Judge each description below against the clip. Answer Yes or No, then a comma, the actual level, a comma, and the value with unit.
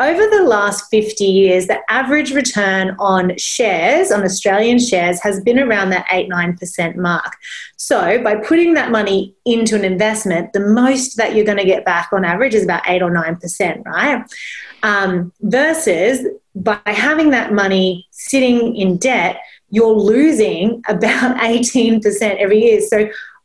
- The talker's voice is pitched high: Yes, high, 215 Hz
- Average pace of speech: Yes, average, 160 wpm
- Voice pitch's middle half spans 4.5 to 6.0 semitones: No, average, 4.0 semitones